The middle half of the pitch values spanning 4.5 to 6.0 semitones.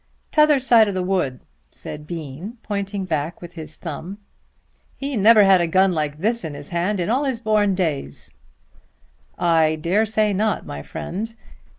Yes: average, 5.1 semitones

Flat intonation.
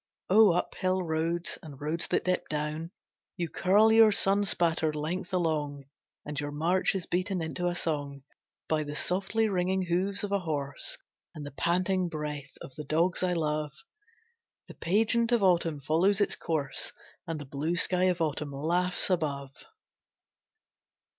No: average, 3.5 semitones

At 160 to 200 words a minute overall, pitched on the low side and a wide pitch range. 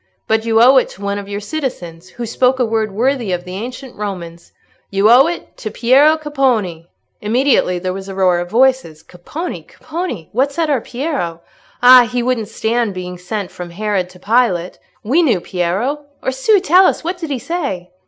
No: average, 185 wpm; high, 225 Hz; wide, 6.3 semitones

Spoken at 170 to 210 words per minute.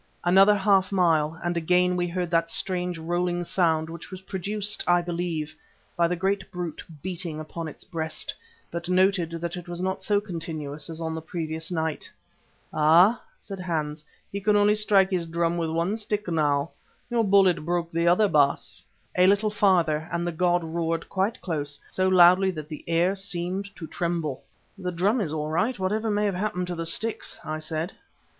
Yes: average, 185 wpm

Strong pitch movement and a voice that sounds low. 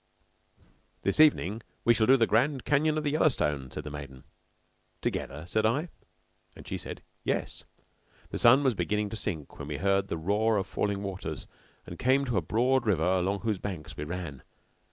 Yes: wide, 6.1 semitones; low, 100 Hz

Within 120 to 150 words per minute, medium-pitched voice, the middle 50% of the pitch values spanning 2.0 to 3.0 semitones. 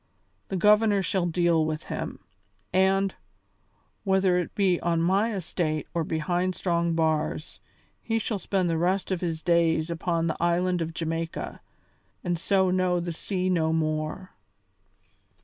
Yes: average, 145 wpm; medium, 175 Hz; narrow, 2.4 semitones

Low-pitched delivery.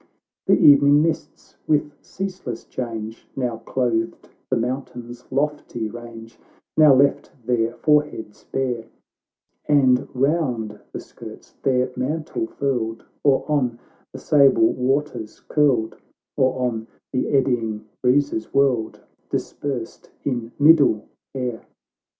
Yes: low, 130 Hz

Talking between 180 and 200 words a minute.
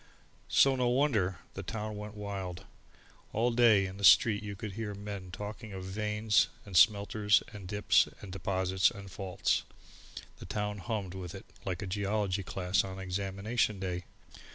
No: average, 160 wpm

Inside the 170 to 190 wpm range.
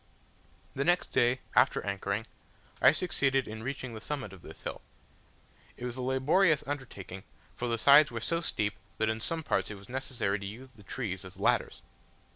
Yes: average, 185 wpm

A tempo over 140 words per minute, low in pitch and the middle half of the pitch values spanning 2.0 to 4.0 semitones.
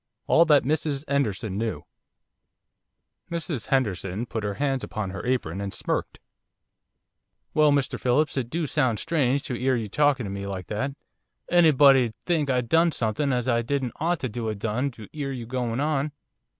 No: average, 170 wpm; low, 130 Hz; average, 4.6 semitones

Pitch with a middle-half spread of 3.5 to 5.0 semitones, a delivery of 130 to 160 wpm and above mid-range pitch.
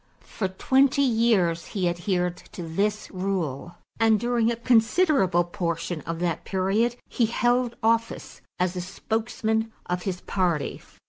Yes: average, 4.6 semitones; slow, 135 wpm; high, 195 Hz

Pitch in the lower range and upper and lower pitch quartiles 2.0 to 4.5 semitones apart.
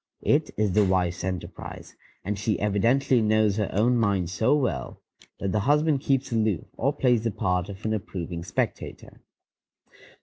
Yes: low, 105 Hz; average, 4.1 semitones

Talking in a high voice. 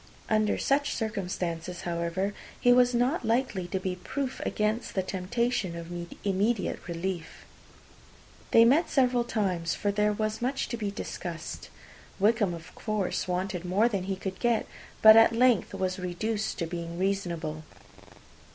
Yes: high, 200 Hz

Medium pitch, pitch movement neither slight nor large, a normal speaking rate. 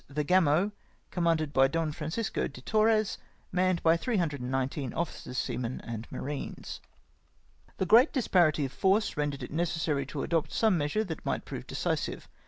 Yes: medium, 160 Hz; average, 4.9 semitones; average, 155 wpm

